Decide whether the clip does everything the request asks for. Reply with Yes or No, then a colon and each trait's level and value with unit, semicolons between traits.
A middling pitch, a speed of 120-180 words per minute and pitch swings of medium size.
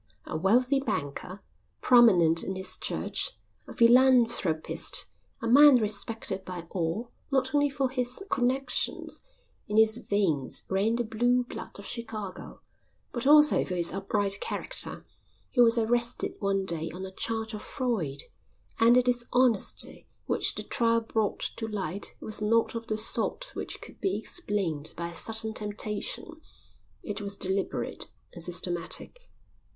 No: high, 220 Hz; average, 145 wpm; average, 4.2 semitones